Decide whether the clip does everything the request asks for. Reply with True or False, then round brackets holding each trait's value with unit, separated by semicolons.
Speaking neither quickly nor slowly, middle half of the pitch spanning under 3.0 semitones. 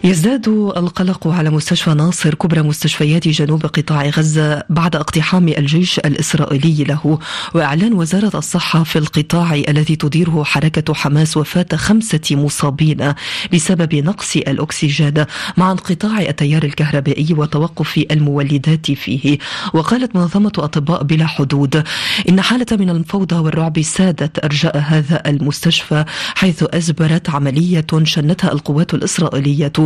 True (115 wpm; 2.6 semitones)